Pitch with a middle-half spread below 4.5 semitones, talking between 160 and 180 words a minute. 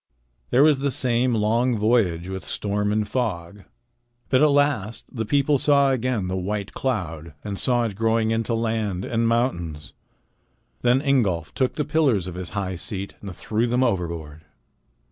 No: average, 5.0 semitones; average, 165 wpm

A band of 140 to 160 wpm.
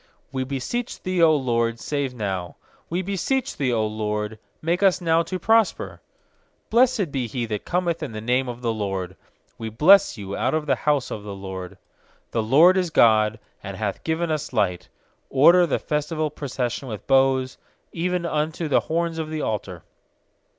No: average, 175 wpm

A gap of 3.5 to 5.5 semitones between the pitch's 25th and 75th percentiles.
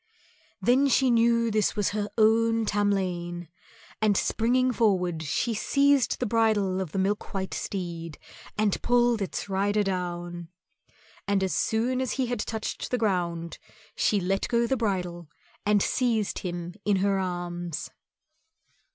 Yes: average, 4.2 semitones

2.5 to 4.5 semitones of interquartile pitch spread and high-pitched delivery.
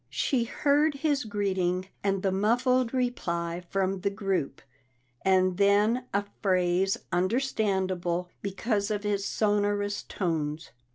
Yes: average, 2.8 semitones; high, 200 Hz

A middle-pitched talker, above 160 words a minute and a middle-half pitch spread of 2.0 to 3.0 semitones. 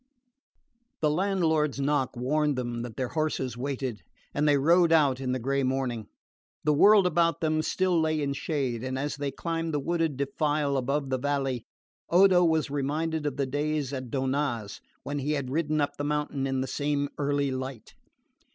Yes: medium, 145 Hz; average, 180 wpm; average, 2.7 semitones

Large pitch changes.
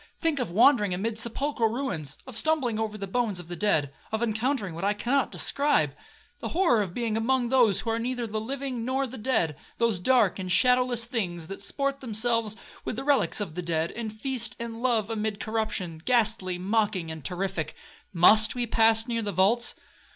No: average, 4.1 semitones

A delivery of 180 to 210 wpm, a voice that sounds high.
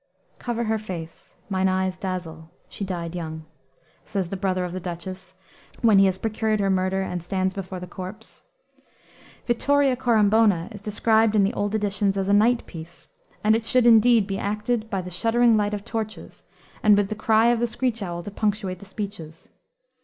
Yes: average, 185 wpm; high, 200 Hz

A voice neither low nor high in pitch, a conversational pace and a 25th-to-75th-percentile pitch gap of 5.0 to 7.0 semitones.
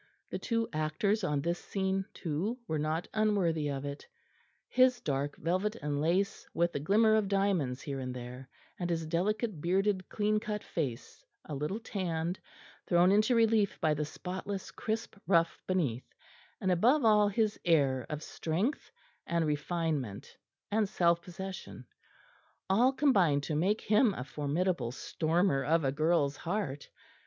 Yes: medium, 175 Hz; average, 150 wpm; wide, 5.6 semitones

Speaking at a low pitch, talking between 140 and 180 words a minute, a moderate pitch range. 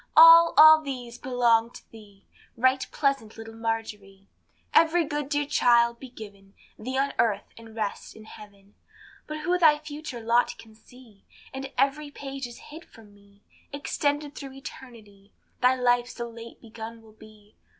No: high, 240 Hz; average, 160 wpm; average, 4.3 semitones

